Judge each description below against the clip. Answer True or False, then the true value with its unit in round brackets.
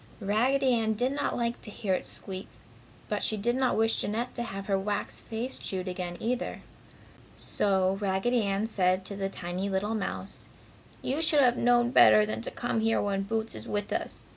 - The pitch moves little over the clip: False (3.6 semitones)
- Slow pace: False (190 wpm)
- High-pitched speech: True (215 Hz)